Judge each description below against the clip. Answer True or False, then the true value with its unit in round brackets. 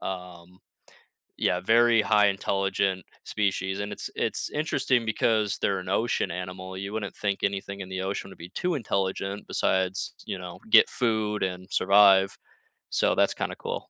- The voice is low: True (95 Hz)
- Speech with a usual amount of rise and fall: False (2.0 semitones)